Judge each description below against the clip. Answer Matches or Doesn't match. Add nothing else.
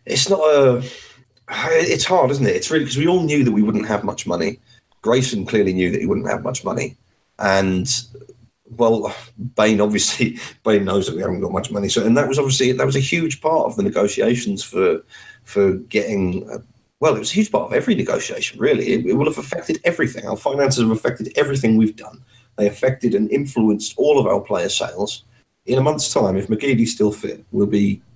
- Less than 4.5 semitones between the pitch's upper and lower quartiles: Doesn't match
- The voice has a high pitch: Doesn't match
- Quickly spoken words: Matches